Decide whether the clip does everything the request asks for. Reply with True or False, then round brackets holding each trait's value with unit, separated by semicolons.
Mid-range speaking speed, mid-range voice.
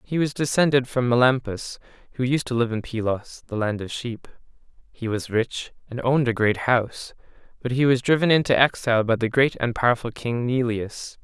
False (190 wpm; 125 Hz)